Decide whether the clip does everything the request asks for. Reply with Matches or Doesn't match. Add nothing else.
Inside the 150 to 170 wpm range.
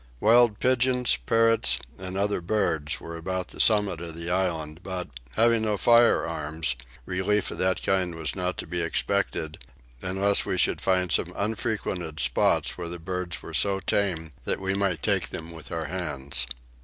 Matches